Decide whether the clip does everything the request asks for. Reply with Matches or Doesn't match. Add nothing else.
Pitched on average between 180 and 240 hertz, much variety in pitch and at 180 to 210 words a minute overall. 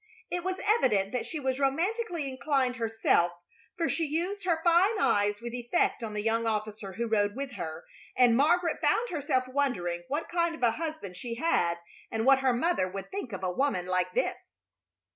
Doesn't match